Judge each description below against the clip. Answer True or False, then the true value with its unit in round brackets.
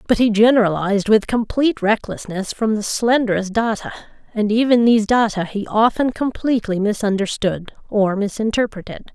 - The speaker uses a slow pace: True (130 wpm)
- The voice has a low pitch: False (215 Hz)